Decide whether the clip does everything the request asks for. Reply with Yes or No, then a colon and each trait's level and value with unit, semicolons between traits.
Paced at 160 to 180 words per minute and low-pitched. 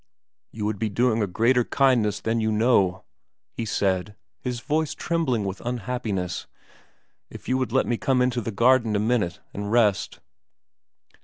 Yes: average, 170 wpm; low, 115 Hz